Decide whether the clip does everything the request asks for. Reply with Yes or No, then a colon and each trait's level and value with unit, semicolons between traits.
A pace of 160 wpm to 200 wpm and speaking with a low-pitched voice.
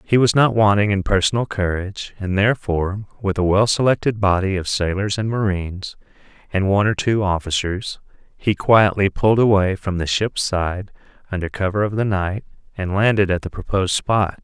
Yes: average, 175 wpm; low, 100 Hz